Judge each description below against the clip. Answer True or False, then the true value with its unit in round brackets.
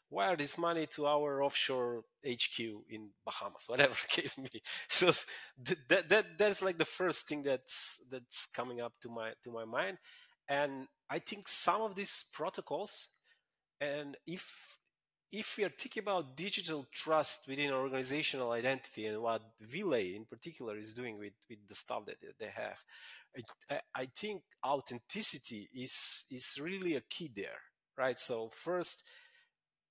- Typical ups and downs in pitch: False (6.9 semitones)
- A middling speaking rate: True (155 wpm)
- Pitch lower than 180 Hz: True (140 Hz)